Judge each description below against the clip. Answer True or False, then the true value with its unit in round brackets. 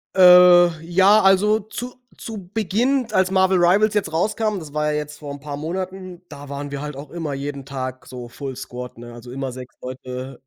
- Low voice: False (160 Hz)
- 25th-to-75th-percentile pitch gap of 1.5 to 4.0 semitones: False (5.6 semitones)